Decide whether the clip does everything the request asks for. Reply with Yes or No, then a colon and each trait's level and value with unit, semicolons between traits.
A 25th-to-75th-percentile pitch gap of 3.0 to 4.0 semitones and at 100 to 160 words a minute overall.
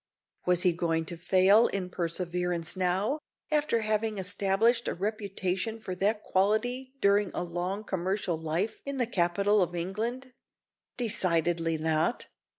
Yes: average, 3.7 semitones; slow, 135 wpm